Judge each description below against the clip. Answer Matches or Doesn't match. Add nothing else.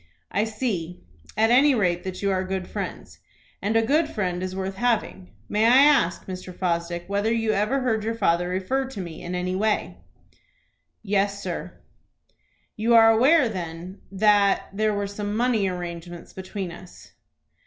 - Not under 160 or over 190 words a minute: Matches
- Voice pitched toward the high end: Matches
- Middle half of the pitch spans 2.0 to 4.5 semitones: Matches